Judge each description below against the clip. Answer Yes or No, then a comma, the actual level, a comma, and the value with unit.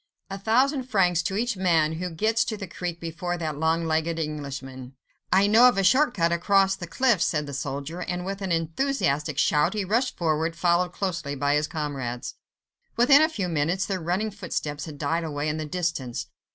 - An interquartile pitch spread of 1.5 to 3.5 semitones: No, average, 4.3 semitones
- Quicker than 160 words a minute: Yes, average, 190 wpm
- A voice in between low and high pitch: Yes, medium, 170 Hz